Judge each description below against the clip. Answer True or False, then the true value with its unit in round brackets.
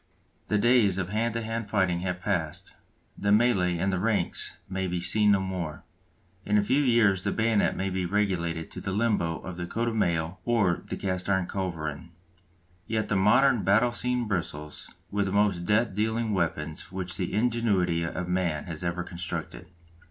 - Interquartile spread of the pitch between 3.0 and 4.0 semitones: True (3.6 semitones)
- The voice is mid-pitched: False (95 Hz)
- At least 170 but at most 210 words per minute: True (180 wpm)